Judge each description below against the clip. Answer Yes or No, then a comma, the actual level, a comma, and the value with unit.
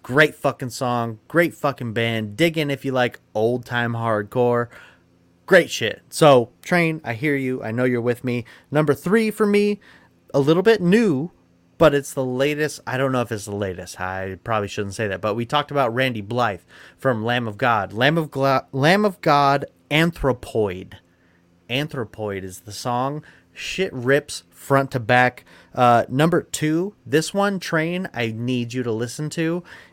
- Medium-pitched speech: No, low, 130 Hz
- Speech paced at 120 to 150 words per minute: No, average, 175 wpm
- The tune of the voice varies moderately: Yes, average, 4.8 semitones